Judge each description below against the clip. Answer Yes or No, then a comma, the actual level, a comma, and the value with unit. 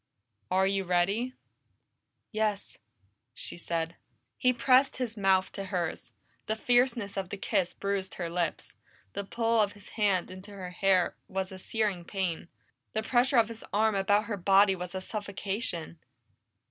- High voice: Yes, high, 200 Hz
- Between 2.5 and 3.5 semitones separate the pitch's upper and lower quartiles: Yes, average, 2.9 semitones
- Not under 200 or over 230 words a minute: No, average, 155 wpm